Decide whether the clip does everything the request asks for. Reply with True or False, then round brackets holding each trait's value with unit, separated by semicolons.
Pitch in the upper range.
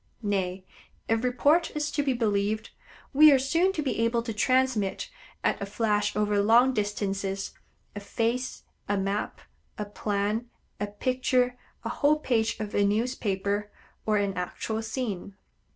True (220 Hz)